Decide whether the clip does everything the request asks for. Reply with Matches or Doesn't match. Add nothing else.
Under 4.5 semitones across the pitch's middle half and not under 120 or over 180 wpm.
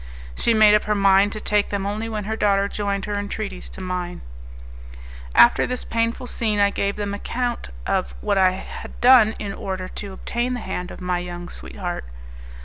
Doesn't match